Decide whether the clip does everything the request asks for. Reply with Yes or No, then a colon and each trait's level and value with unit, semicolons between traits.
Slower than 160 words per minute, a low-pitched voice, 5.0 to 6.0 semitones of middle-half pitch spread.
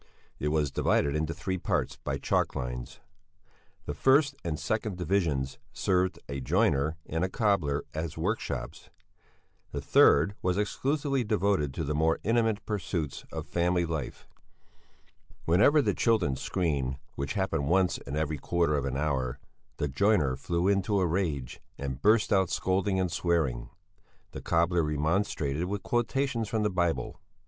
Yes: average, 150 wpm; very low, 85 Hz; wide, 5.6 semitones